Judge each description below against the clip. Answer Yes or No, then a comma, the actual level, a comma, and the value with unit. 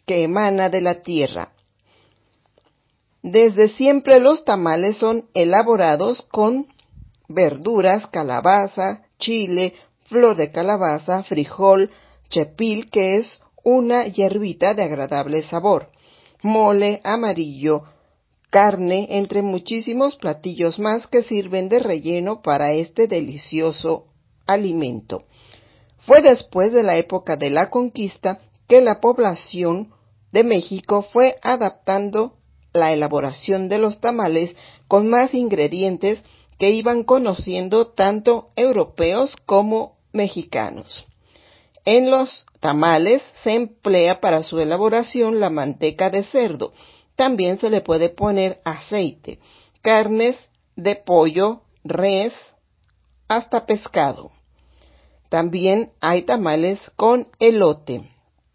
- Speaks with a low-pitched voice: No, high, 195 Hz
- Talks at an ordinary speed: No, slow, 105 wpm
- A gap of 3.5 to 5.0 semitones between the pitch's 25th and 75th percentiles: No, wide, 5.5 semitones